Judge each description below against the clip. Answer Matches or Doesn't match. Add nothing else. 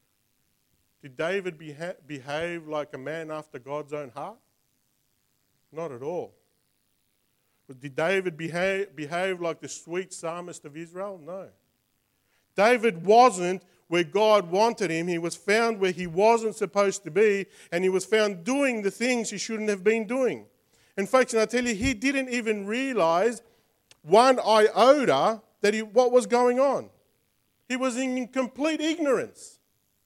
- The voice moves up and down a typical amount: Doesn't match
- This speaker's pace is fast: Doesn't match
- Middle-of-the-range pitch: Doesn't match